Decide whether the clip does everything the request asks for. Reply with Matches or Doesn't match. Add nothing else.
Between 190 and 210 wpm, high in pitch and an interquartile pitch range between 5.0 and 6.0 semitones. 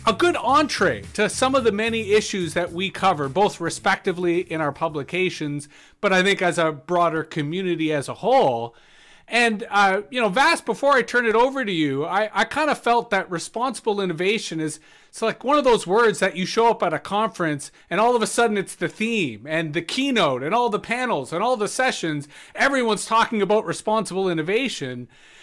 Matches